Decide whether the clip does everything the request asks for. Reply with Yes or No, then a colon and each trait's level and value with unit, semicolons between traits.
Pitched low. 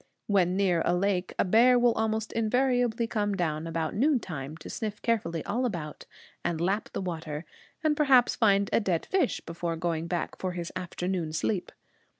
No: high, 190 Hz